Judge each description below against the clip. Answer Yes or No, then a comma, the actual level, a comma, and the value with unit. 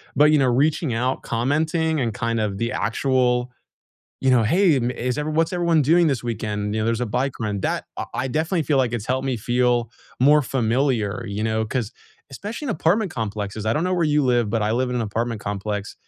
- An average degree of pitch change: Yes, average, 4.9 semitones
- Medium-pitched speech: No, low, 125 Hz